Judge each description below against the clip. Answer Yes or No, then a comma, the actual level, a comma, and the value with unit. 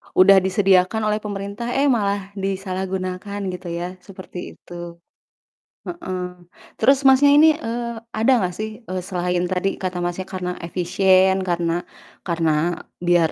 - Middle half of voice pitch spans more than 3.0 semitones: No, average, 2.7 semitones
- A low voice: No, medium, 185 Hz